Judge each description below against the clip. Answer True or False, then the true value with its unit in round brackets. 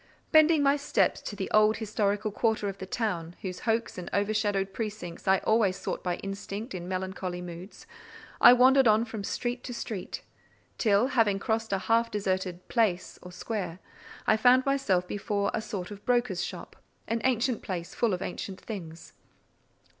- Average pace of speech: True (170 wpm)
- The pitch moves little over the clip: False (3.6 semitones)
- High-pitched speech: True (205 Hz)